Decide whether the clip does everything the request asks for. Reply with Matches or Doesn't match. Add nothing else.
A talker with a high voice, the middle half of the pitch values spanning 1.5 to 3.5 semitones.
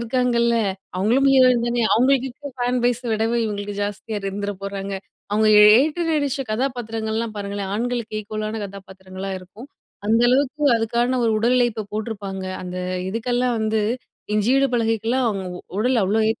Matches